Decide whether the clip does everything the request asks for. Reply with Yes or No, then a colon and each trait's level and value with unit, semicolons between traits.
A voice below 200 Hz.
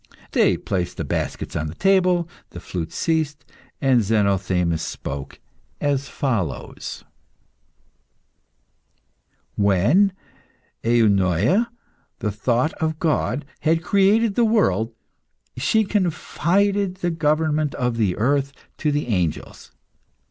Yes: medium, 140 Hz